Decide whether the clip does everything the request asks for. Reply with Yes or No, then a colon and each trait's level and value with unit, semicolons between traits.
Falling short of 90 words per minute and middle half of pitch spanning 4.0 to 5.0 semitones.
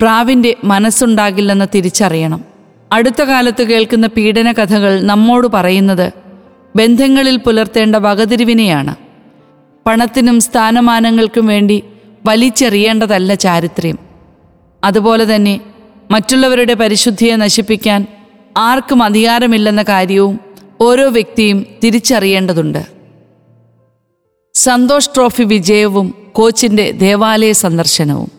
No: average, 75 wpm; average, 2.9 semitones